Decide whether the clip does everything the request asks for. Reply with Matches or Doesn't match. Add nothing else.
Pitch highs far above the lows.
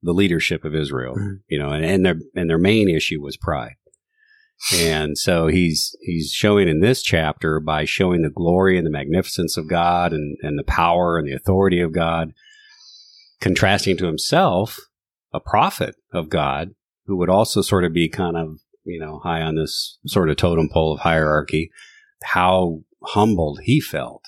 Doesn't match